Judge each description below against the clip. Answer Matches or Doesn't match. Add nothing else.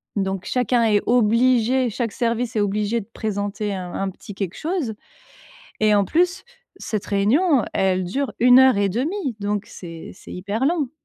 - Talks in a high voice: Matches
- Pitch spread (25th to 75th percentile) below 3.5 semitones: Doesn't match